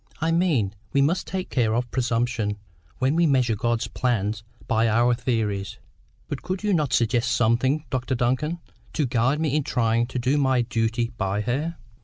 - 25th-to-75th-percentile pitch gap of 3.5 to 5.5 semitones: Yes, average, 3.8 semitones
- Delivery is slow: No, average, 175 wpm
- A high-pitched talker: No, low, 125 Hz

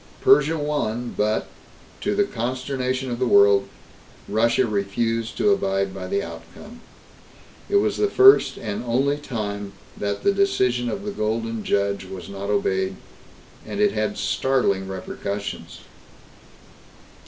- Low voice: Yes, low, 115 Hz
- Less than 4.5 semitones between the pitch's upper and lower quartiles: No, average, 5.2 semitones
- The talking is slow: Yes, slow, 130 wpm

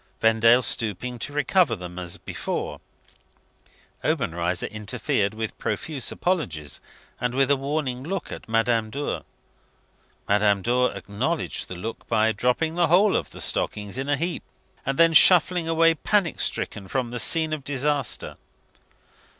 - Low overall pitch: Yes, low, 125 Hz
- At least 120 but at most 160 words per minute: Yes, average, 140 wpm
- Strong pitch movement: Yes, wide, 6.6 semitones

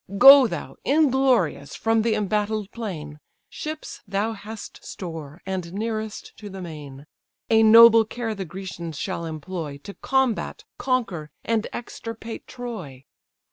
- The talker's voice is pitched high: Yes, high, 210 Hz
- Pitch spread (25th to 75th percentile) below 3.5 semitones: No, average, 5.2 semitones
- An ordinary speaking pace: No, slow, 130 wpm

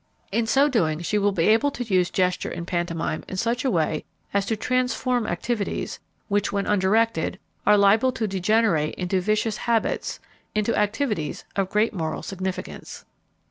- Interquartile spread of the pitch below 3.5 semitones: No, average, 3.8 semitones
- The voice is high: Yes, high, 205 Hz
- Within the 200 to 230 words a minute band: No, average, 160 wpm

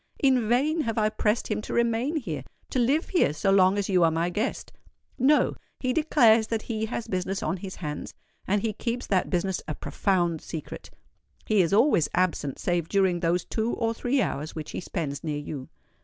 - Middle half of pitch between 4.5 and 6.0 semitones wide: Yes, average, 5.2 semitones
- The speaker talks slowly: No, average, 190 wpm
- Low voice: No, high, 200 Hz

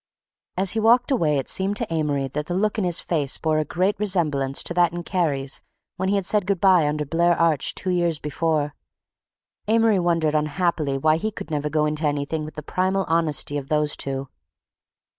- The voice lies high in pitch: No, medium, 165 Hz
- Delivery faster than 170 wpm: Yes, average, 200 wpm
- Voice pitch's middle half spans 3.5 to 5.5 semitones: Yes, average, 3.8 semitones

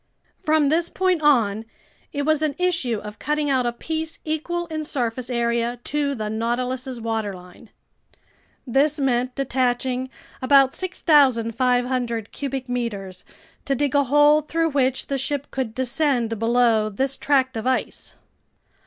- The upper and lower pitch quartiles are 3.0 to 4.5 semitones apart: Yes, average, 3.7 semitones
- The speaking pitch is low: No, very high, 260 Hz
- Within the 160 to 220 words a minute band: No, slow, 135 wpm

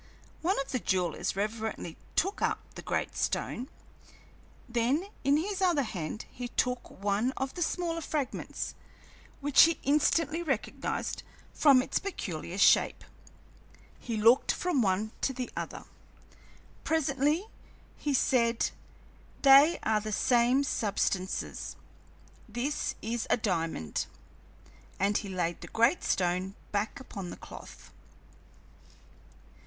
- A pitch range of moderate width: No, wide, 6.0 semitones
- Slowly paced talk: Yes, slow, 120 wpm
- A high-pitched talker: Yes, high, 245 Hz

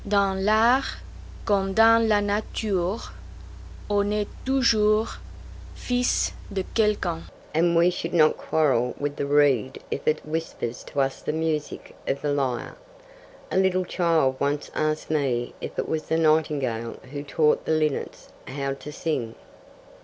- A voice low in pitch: No, medium, 160 Hz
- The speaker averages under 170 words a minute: Yes, average, 145 wpm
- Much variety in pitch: Yes, wide, 5.9 semitones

